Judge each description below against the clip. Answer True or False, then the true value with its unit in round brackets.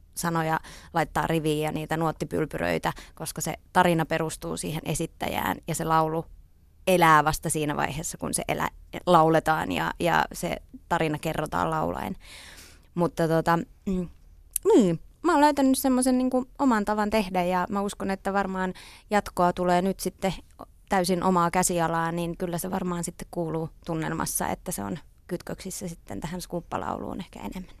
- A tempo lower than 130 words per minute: False (145 wpm)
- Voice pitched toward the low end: False (175 Hz)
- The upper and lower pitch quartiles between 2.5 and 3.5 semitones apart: True (2.9 semitones)